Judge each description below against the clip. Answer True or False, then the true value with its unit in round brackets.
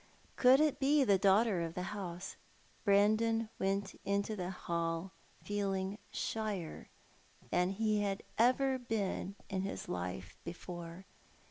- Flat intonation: False (3.5 semitones)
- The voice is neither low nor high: False (195 Hz)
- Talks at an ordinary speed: False (125 wpm)